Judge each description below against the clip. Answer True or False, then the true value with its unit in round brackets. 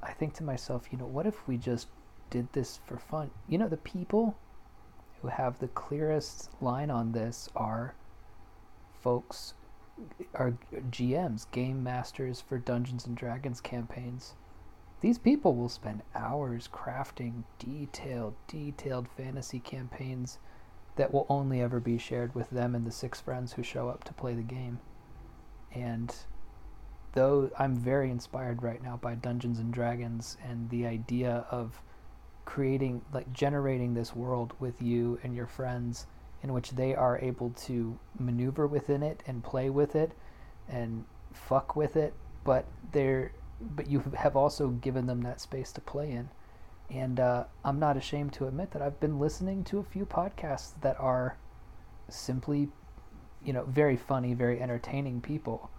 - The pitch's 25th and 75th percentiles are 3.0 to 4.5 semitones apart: False (2.5 semitones)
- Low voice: True (125 Hz)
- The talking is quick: False (155 wpm)